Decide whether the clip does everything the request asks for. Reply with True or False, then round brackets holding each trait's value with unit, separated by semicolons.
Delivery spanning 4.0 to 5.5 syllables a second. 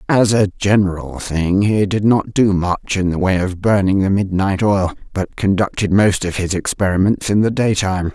True (4.8 syllables/s)